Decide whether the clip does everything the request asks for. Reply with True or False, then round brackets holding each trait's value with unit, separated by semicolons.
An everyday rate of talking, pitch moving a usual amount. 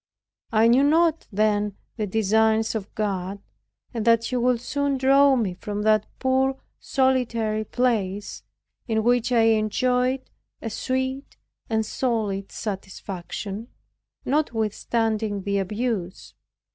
False (115 wpm; 3.4 semitones)